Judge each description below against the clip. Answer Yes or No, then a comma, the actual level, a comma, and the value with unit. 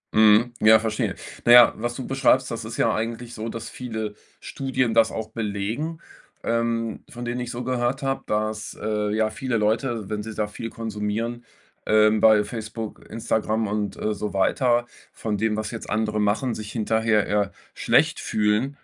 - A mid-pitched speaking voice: No, low, 110 Hz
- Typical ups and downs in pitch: No, narrow, 2.0 semitones